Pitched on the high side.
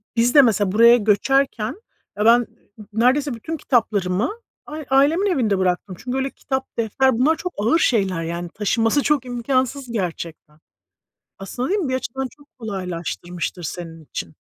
Yes: high, 230 Hz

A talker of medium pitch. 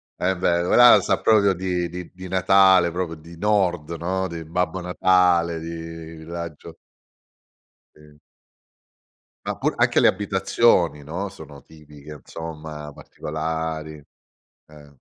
No: very low, 85 Hz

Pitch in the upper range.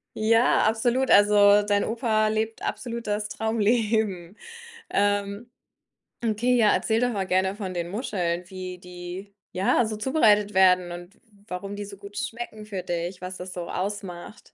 Yes: high, 205 Hz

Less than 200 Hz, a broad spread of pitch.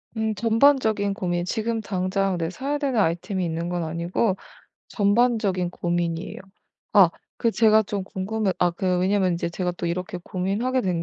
No: high, 190 Hz; average, 3.8 semitones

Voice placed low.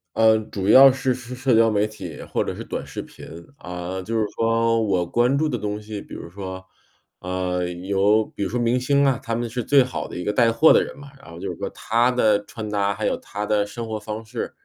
Yes: low, 110 Hz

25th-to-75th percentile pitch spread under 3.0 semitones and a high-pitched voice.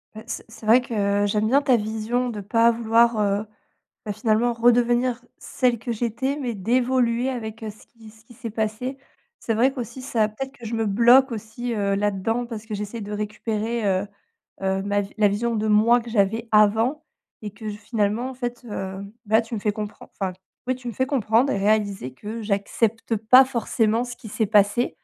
Yes: narrow, 2.4 semitones; high, 225 Hz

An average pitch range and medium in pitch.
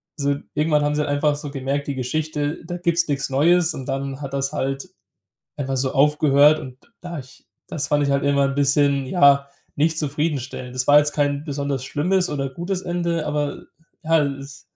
No: narrow, 2.0 semitones; medium, 145 Hz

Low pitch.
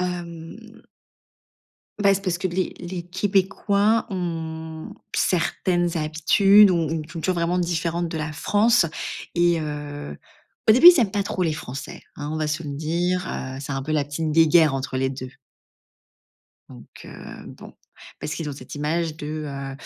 No: medium, 165 Hz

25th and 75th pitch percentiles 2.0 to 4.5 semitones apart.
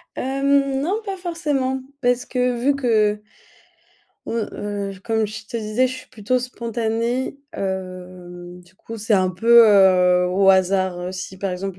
No: average, 5.2 semitones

